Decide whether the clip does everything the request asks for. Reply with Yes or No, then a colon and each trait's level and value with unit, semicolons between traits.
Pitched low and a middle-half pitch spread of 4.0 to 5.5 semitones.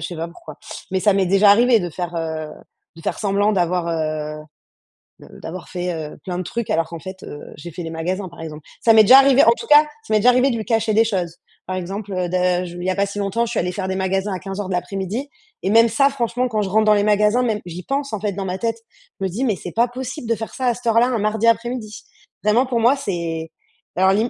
No: high, 200 Hz; average, 4.4 semitones